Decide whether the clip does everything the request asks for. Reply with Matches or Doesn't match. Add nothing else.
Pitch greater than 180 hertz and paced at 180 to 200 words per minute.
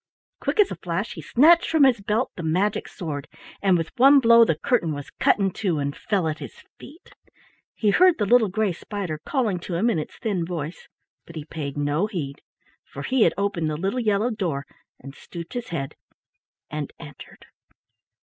Matches